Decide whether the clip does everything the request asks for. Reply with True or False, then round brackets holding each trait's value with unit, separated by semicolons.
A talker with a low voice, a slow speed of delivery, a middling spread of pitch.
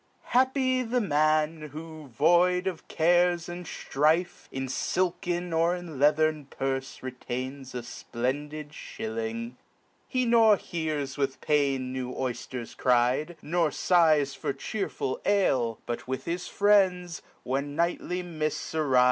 False (155 Hz; 120 wpm; 4.9 semitones)